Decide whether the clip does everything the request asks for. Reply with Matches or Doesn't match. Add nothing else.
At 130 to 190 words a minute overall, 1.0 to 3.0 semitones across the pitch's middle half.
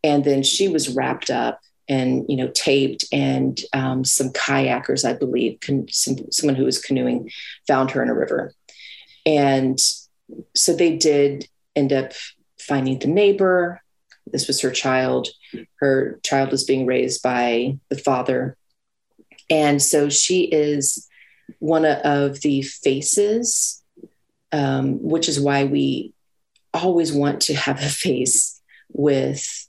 Matches